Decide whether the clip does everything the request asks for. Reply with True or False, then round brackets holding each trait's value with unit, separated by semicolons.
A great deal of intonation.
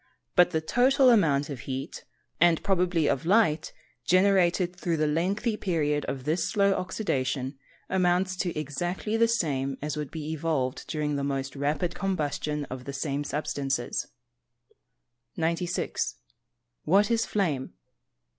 False (4.5 semitones)